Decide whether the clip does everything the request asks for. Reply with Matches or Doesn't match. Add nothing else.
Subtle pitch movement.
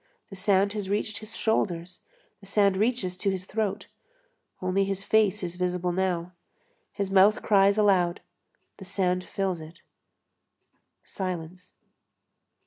Matches